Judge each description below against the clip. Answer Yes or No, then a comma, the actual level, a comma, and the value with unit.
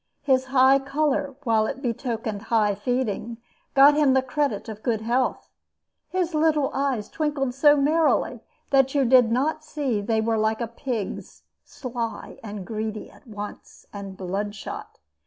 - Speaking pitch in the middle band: No, very high, 250 Hz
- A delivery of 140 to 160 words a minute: Yes, average, 150 wpm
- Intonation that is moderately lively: Yes, average, 4.1 semitones